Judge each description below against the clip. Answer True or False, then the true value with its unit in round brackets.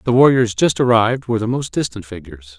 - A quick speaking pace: True (210 wpm)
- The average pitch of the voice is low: True (110 Hz)